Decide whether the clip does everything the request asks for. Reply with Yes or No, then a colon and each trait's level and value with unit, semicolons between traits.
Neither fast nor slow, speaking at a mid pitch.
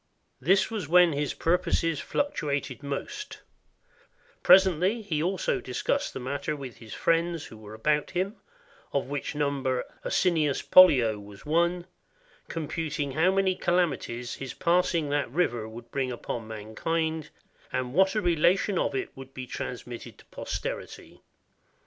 Yes: average, 145 wpm; medium, 150 Hz